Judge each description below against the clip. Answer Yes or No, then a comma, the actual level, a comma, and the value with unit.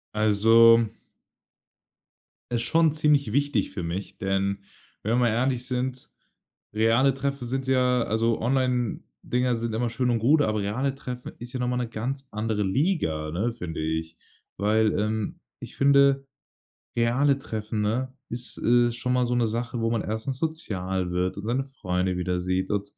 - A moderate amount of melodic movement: Yes, average, 3.6 semitones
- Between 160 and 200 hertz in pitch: No, low, 115 Hz